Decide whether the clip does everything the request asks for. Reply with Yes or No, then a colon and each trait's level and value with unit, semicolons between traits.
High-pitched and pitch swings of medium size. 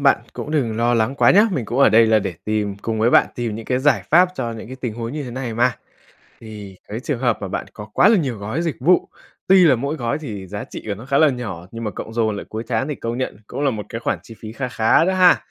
No: low, 120 Hz; average, 4.1 semitones